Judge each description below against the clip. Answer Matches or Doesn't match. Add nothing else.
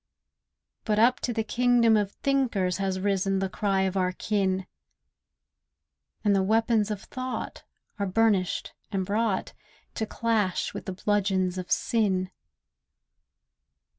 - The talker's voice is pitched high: Matches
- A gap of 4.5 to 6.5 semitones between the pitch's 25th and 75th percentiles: Doesn't match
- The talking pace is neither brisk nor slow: Doesn't match